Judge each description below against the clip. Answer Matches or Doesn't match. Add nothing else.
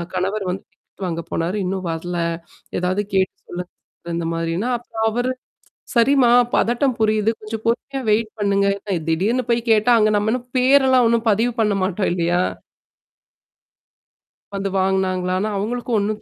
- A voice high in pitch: Matches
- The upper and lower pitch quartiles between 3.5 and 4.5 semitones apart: Matches